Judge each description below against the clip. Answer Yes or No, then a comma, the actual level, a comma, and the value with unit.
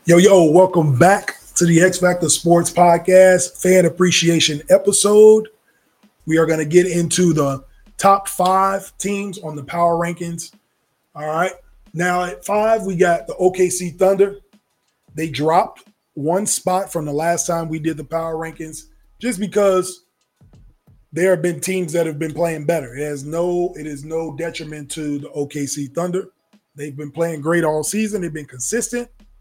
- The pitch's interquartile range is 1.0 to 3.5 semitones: Yes, average, 2.9 semitones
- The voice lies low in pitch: No, medium, 175 Hz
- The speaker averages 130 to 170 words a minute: Yes, average, 165 wpm